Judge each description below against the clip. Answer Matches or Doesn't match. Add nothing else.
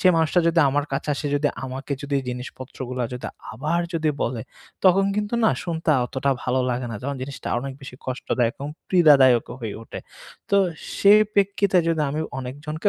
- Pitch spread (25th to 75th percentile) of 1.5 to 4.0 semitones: Doesn't match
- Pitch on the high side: Doesn't match